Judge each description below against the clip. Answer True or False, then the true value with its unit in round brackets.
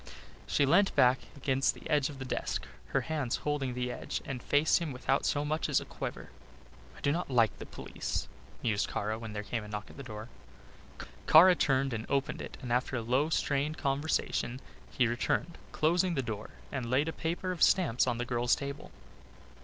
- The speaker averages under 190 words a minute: False (200 wpm)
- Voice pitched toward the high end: False (135 Hz)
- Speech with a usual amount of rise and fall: True (3.9 semitones)